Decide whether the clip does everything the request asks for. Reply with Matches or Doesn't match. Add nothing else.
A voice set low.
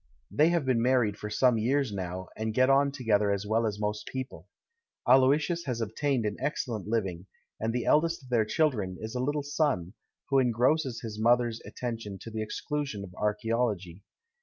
Matches